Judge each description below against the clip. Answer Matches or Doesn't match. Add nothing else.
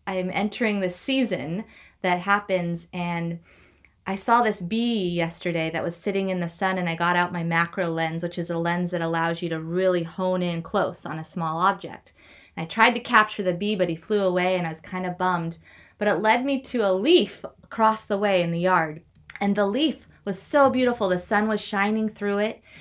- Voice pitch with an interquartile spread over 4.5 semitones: Doesn't match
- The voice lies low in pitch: Doesn't match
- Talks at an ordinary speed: Doesn't match